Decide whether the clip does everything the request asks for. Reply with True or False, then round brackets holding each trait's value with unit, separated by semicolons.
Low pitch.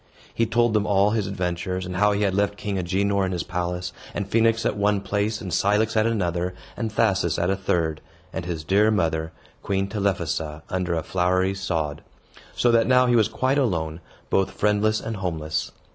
True (95 Hz)